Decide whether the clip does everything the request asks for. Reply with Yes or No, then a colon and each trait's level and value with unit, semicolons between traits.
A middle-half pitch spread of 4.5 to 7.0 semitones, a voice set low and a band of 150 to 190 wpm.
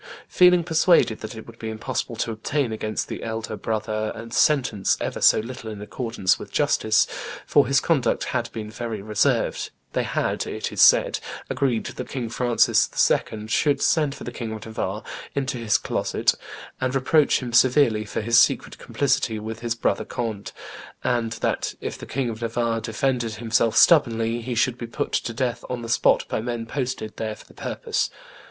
No: narrow, 2.6 semitones; low, 115 Hz; average, 185 wpm